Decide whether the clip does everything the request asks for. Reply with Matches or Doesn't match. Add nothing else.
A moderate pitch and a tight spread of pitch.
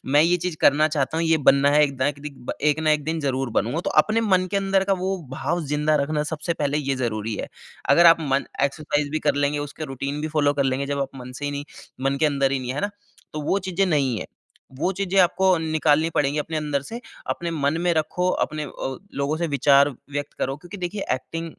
Doesn't match